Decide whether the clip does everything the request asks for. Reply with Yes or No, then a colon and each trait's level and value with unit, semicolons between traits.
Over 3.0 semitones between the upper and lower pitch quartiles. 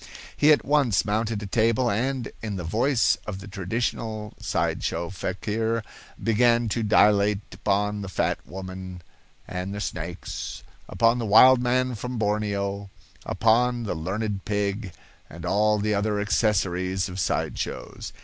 No: average, 2.7 semitones